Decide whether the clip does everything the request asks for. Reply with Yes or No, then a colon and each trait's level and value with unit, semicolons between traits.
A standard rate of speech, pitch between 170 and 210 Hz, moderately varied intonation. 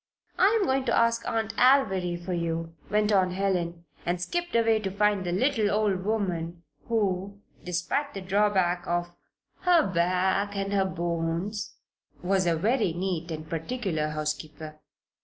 Yes: average, 145 wpm; high, 190 Hz; average, 3.7 semitones